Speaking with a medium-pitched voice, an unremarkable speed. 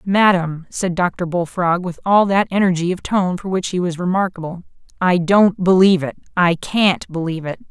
Yes: medium, 180 Hz; average, 170 wpm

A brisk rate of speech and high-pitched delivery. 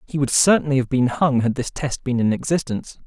No: fast, 235 wpm; low, 135 Hz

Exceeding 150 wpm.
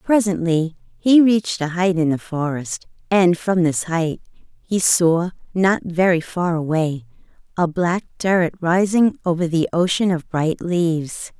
No: average, 145 wpm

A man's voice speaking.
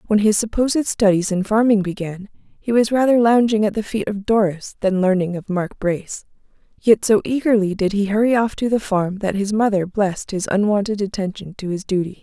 No: female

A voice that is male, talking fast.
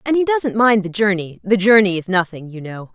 No: female; fast, 245 wpm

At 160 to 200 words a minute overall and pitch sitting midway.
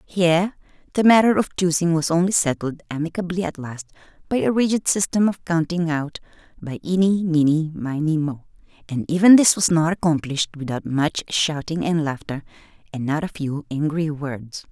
Yes: average, 165 wpm; medium, 165 Hz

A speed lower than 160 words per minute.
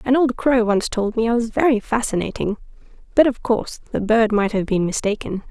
No: fast, 205 wpm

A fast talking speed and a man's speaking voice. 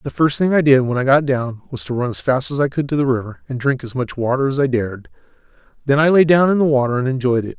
Yes: fast, 300 wpm; male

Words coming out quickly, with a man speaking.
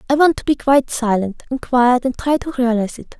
No: fast, 245 wpm; female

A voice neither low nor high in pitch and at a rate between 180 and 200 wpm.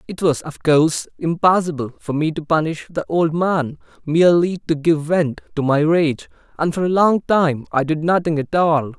Yes: medium, 160 Hz; average, 195 wpm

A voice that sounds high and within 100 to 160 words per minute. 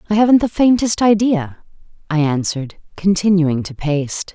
No: medium, 180 Hz; average, 140 wpm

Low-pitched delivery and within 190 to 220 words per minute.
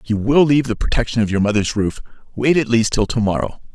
No: low, 115 Hz; fast, 240 wpm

